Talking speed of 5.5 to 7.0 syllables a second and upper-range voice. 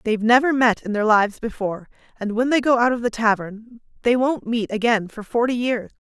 Yes: 5.9 syllables/s; high, 230 Hz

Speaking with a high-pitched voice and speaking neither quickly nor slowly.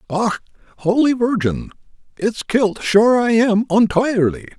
No: high, 215 Hz; slow, 120 wpm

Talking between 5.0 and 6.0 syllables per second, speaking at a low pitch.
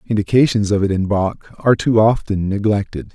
Yes: 5.6 syllables/s; low, 105 Hz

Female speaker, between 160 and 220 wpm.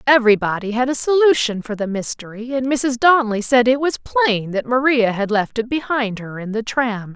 Yes: female; average, 200 wpm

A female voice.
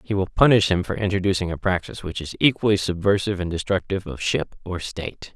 No: male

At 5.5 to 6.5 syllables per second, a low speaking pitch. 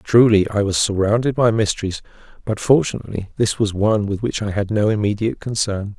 Yes: 5.9 syllables/s; low, 105 Hz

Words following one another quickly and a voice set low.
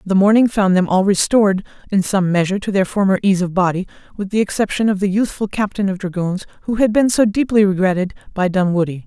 No: fast, 210 wpm; high, 195 Hz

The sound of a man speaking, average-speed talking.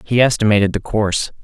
Yes: male; average, 170 wpm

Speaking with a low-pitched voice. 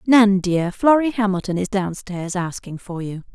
No: high, 195 Hz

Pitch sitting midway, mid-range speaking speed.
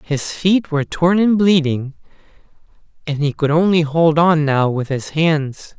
Yes: medium, 160 Hz; average, 165 wpm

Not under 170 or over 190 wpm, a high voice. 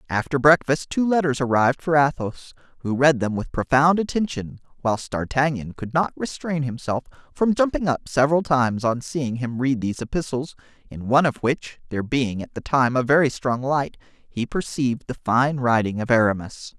No: average, 180 wpm; low, 135 Hz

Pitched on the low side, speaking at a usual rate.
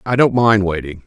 No: low, 105 Hz; fast, 225 wpm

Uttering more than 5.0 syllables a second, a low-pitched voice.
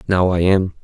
No: 4.9 syllables/s; very low, 90 Hz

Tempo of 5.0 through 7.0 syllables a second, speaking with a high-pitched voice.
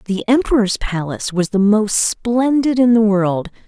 No: 4.5 syllables/s; high, 215 Hz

